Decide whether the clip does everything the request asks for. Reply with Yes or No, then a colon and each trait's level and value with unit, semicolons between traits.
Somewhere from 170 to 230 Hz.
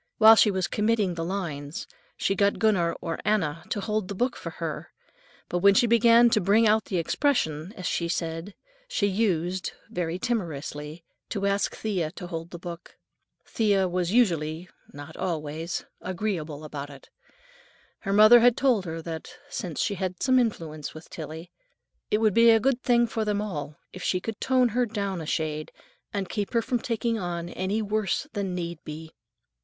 Yes: high, 190 Hz